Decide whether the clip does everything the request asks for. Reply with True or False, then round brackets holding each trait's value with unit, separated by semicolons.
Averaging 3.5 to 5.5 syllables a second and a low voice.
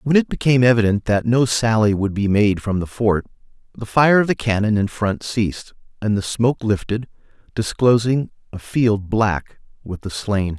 True (4.9 syllables/s; 110 Hz)